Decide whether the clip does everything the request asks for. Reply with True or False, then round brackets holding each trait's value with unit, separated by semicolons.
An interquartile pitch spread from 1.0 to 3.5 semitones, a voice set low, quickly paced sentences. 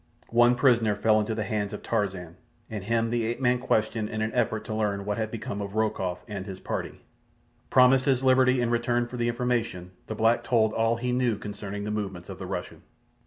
True (2.7 semitones; 110 Hz; 215 wpm)